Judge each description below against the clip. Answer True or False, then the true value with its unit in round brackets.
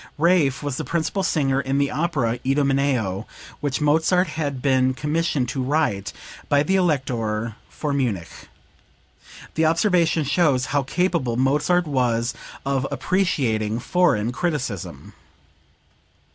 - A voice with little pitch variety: False (4.3 semitones)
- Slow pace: True (115 wpm)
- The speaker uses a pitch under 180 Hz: True (140 Hz)